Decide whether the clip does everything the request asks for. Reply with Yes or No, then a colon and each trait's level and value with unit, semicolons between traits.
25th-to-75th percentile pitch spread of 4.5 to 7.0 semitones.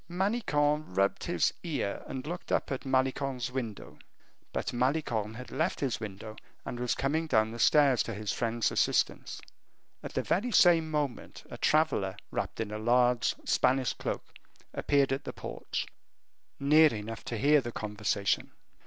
Yes: average, 5.1 semitones